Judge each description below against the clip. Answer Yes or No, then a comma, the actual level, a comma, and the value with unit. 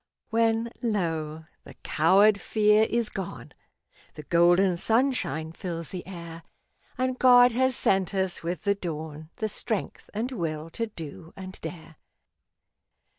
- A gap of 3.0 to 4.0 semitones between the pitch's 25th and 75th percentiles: No, average, 5.3 semitones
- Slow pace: Yes, slow, 130 wpm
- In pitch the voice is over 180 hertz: Yes, high, 190 Hz